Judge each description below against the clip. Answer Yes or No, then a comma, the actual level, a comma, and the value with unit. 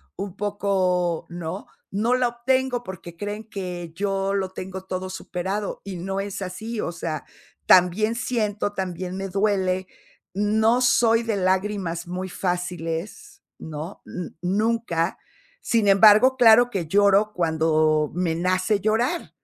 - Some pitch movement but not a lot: Yes, average, 3.2 semitones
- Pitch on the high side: Yes, high, 195 Hz